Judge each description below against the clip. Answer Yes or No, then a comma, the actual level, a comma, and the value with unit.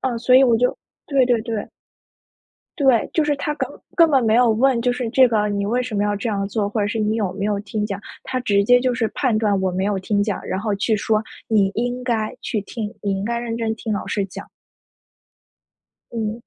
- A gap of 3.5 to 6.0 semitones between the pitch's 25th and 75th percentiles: No, average, 3.1 semitones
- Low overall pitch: No, high, 220 Hz